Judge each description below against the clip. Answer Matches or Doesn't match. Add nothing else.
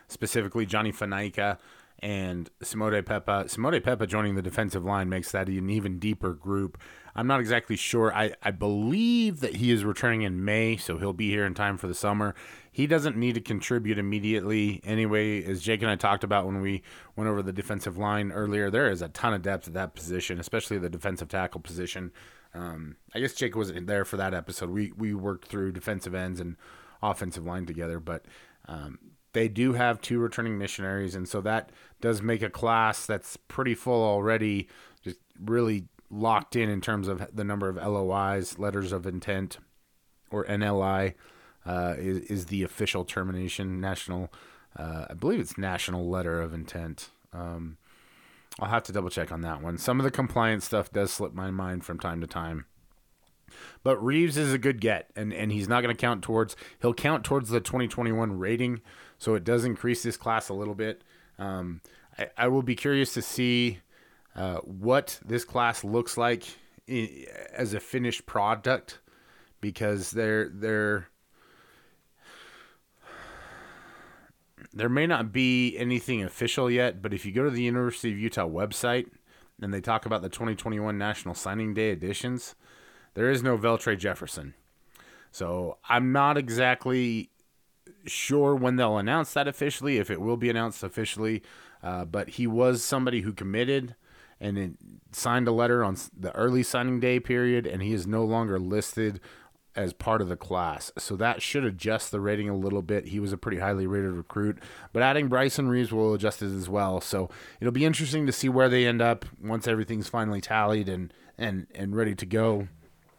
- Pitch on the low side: Matches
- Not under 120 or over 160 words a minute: Doesn't match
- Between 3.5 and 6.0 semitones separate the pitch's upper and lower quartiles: Matches